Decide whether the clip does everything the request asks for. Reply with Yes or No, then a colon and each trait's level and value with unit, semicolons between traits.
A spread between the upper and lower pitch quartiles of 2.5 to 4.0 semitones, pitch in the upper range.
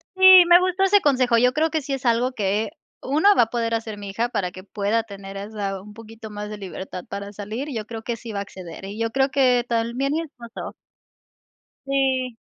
No: average, 4.5 semitones; high, 230 Hz